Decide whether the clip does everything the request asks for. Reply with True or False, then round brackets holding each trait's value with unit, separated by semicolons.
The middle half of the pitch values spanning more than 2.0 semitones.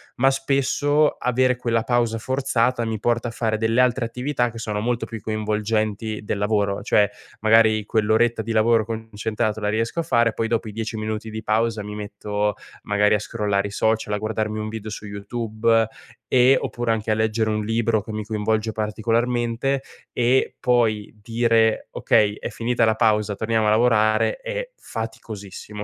False (1.7 semitones)